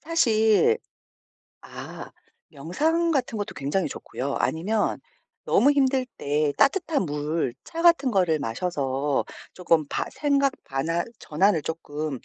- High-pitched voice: No, medium, 180 Hz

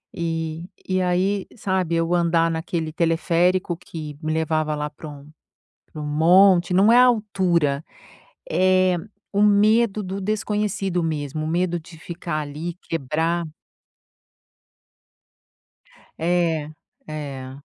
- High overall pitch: No, medium, 170 Hz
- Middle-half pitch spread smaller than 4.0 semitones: Yes, average, 3.0 semitones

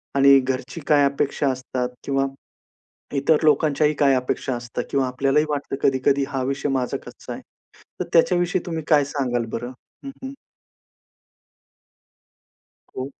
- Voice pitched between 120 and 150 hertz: Yes, medium, 140 Hz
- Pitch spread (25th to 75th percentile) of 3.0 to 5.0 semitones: No, narrow, 2.4 semitones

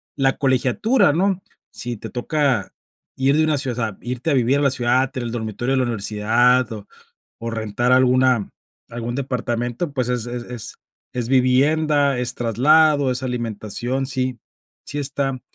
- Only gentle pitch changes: Yes, narrow, 2.3 semitones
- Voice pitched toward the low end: Yes, low, 125 Hz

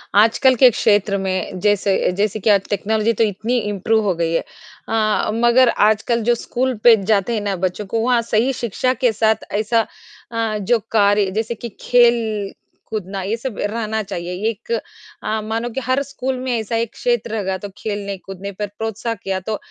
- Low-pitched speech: No, high, 220 Hz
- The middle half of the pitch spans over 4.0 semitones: No, narrow, 2.5 semitones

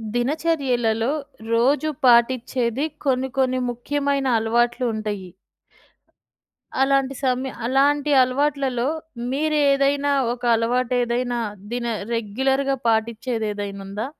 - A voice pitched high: Yes, very high, 255 Hz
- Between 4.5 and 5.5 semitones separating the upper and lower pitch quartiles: No, average, 2.9 semitones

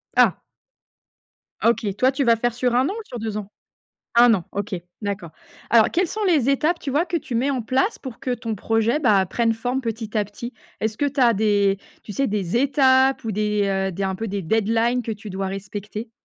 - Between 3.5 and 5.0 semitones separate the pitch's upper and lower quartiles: Yes, average, 4.0 semitones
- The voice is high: Yes, high, 225 Hz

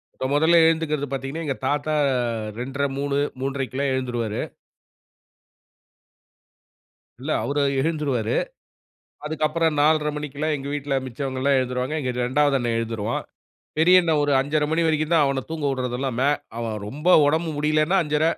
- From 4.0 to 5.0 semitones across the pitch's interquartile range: No, average, 2.7 semitones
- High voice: No, medium, 145 Hz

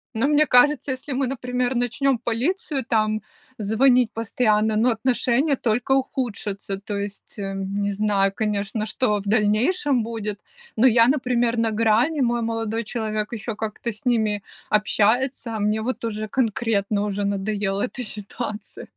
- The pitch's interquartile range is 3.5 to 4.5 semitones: No, average, 3.1 semitones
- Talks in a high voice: Yes, high, 225 Hz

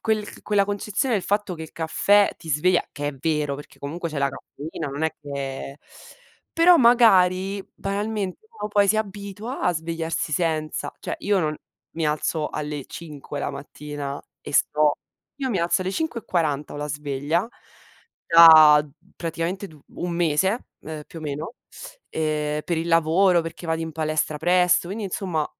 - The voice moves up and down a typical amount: Yes, average, 4.6 semitones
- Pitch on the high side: No, medium, 165 Hz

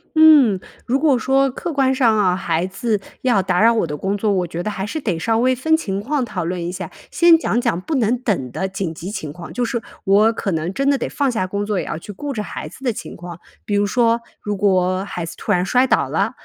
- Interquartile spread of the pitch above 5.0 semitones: Yes, wide, 5.5 semitones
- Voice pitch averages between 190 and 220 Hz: Yes, high, 210 Hz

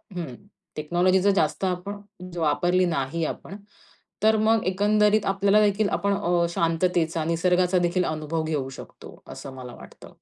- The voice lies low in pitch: No, medium, 180 Hz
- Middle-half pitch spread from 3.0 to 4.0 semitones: Yes, average, 3.5 semitones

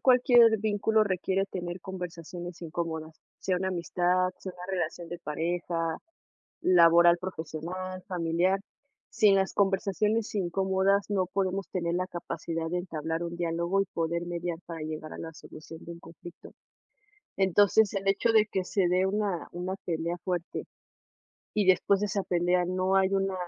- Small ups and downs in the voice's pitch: Yes, narrow, 2.3 semitones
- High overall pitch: No, medium, 180 Hz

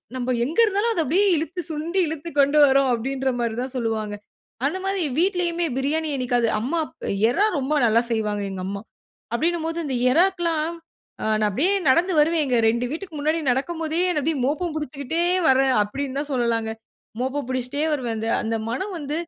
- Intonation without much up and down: No, average, 5.2 semitones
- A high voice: Yes, very high, 285 Hz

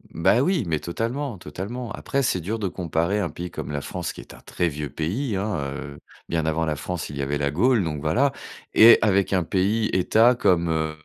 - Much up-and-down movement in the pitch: Yes, wide, 6.1 semitones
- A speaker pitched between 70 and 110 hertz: Yes, very low, 90 Hz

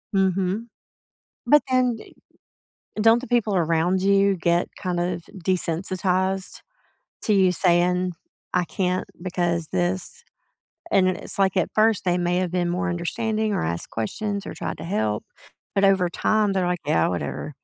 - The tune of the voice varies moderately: No, narrow, 2.3 semitones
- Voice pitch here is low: No, medium, 185 Hz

